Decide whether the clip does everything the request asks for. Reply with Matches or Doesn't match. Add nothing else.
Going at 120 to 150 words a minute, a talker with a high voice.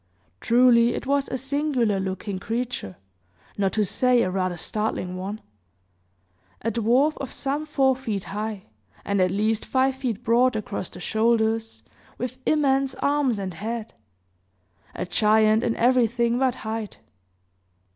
Matches